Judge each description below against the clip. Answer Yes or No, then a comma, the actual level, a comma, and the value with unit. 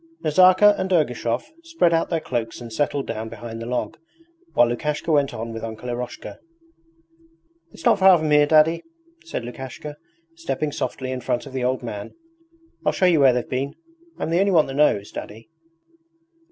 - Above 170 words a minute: Yes, average, 180 wpm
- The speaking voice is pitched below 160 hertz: Yes, medium, 140 Hz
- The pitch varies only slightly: No, wide, 5.5 semitones